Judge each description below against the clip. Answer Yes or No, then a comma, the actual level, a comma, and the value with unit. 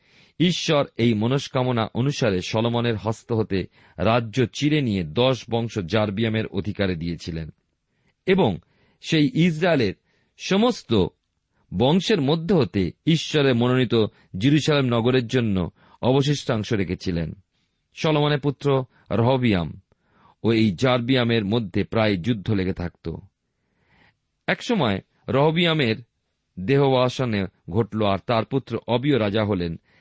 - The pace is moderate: Yes, average, 100 wpm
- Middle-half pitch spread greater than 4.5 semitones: Yes, average, 5.2 semitones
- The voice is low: Yes, low, 115 Hz